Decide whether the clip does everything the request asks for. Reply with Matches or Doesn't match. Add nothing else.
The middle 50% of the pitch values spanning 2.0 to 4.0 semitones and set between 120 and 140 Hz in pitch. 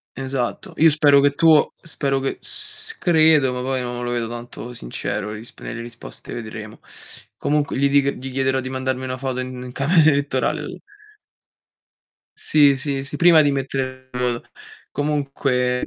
Matches